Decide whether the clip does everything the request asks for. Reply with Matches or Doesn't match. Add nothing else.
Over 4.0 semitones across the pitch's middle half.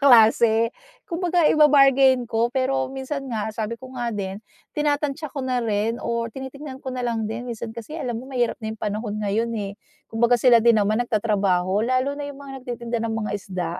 Doesn't match